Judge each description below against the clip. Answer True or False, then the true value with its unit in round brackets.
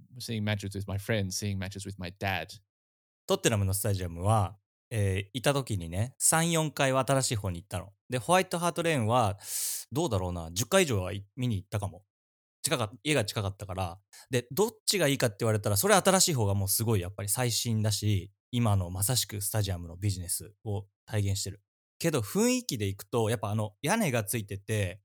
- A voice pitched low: True (105 Hz)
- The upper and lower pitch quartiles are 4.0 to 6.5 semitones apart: True (4.5 semitones)